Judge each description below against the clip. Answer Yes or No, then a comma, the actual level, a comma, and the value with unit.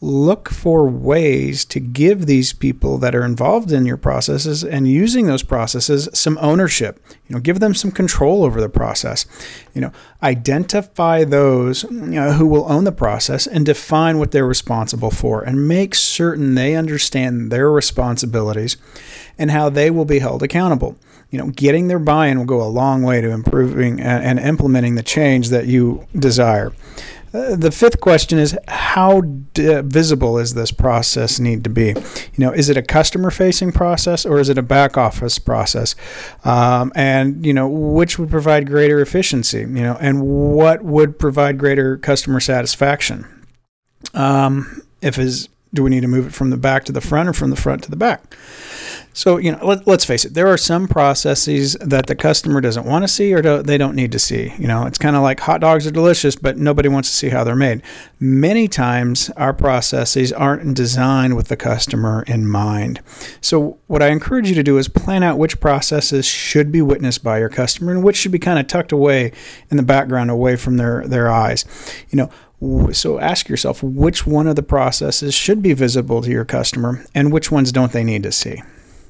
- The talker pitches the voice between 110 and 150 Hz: Yes, medium, 140 Hz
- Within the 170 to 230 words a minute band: Yes, average, 195 wpm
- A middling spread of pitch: Yes, average, 3.9 semitones